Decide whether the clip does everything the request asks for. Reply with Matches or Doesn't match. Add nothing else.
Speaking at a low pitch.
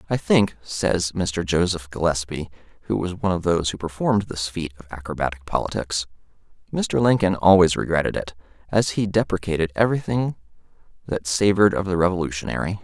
Matches